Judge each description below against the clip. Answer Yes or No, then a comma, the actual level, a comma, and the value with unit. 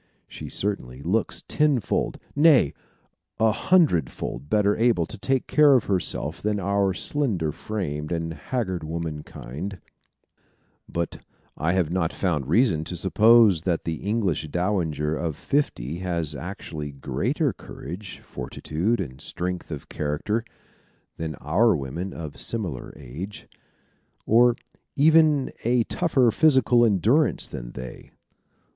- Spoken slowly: Yes, slow, 120 wpm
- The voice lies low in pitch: Yes, very low, 90 Hz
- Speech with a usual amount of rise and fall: No, wide, 6.7 semitones